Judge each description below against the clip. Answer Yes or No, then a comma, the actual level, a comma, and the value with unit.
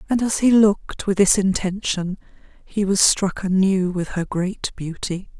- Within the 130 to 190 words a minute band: Yes, average, 165 wpm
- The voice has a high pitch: Yes, high, 195 Hz